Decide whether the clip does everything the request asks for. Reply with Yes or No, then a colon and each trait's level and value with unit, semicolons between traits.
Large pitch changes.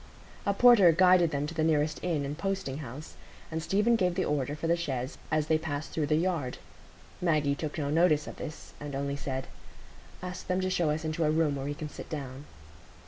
No: average, 3.2 semitones